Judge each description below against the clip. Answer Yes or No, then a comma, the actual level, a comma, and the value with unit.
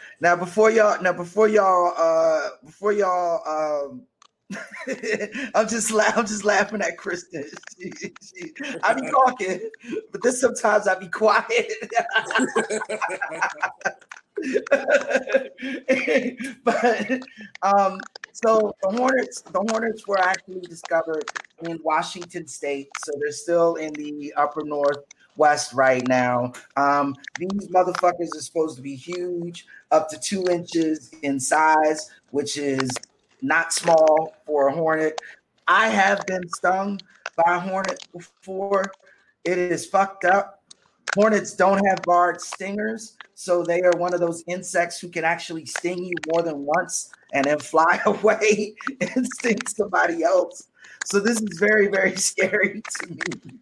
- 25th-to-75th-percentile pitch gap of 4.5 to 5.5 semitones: Yes, average, 4.8 semitones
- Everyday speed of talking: No, slow, 130 wpm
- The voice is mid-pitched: Yes, medium, 180 Hz